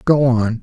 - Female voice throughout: No, male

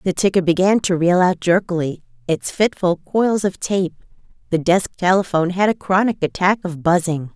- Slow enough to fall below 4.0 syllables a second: No, 5.1 syllables/s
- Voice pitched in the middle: Yes, medium, 180 Hz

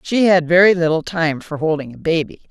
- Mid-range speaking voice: Yes, medium, 165 Hz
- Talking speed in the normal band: No, fast, 215 wpm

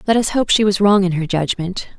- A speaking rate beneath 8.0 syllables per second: Yes, 6.3 syllables/s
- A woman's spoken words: Yes, female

